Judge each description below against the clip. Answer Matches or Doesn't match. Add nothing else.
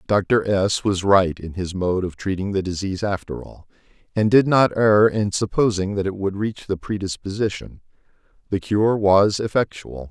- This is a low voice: Matches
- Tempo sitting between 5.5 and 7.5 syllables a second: Doesn't match